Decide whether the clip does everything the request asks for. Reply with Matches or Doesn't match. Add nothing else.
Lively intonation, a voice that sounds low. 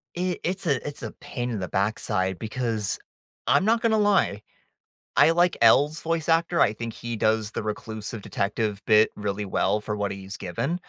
Matches